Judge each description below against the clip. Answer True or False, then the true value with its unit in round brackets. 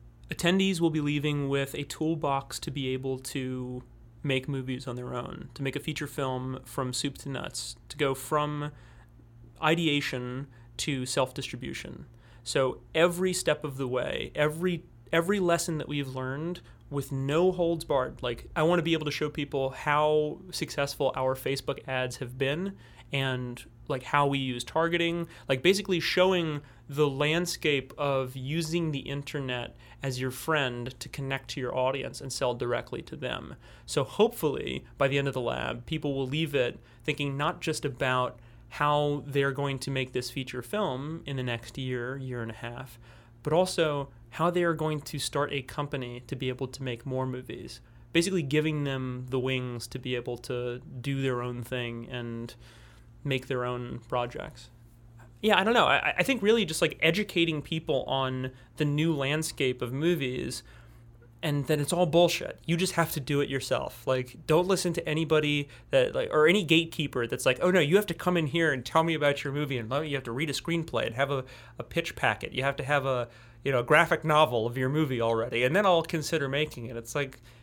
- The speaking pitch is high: False (140 Hz)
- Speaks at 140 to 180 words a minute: False (195 wpm)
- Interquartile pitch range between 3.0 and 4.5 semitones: True (3.9 semitones)